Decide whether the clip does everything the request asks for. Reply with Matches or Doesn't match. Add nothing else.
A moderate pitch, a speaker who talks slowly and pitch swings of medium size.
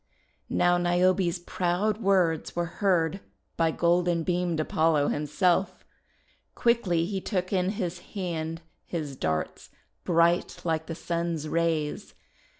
Doesn't match